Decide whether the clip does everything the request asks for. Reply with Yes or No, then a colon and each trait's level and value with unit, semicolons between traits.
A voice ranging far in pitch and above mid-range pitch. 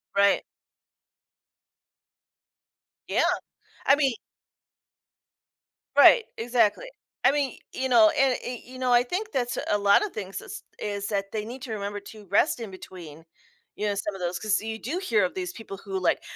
No: average, 4.3 semitones; high, 215 Hz